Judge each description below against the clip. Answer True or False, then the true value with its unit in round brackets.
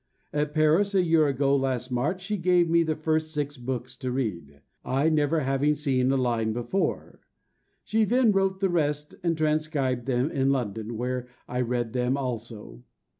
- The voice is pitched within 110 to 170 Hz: True (140 Hz)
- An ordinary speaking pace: True (175 wpm)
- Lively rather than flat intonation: False (4.2 semitones)